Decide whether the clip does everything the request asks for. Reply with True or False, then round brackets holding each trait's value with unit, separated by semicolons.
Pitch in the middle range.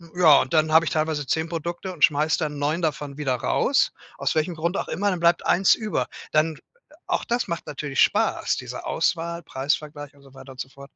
True (155 Hz)